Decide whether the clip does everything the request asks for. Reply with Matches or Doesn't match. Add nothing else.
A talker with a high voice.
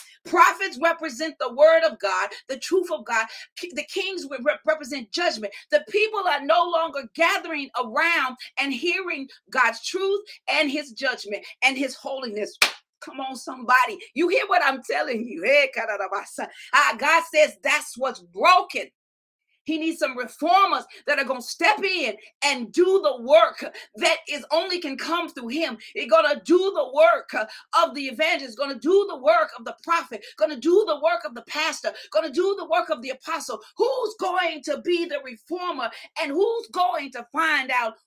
Matches